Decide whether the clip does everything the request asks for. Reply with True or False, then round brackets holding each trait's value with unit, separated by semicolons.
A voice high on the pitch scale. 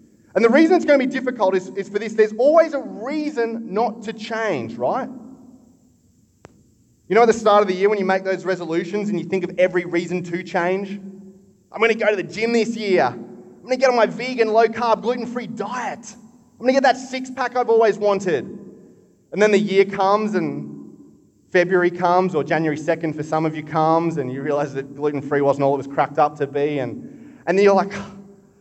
True (200 Hz)